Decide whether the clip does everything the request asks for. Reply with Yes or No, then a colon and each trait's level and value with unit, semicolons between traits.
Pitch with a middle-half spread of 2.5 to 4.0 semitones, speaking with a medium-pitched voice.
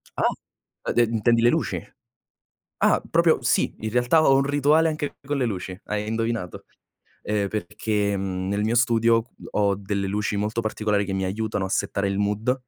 No: average, 2.9 semitones; low, 110 Hz